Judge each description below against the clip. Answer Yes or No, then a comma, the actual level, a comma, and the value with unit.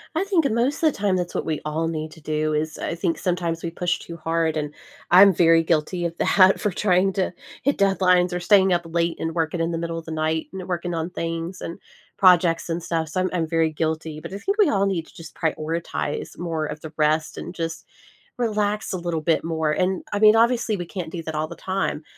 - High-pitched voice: No, medium, 170 Hz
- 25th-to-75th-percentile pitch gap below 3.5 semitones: Yes, average, 2.7 semitones